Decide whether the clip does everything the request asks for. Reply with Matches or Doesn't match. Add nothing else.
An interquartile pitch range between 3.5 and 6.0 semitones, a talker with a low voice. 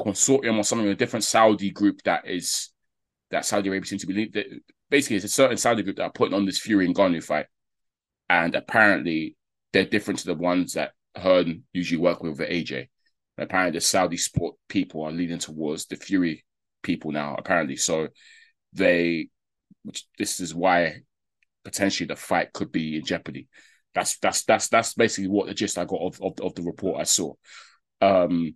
Matches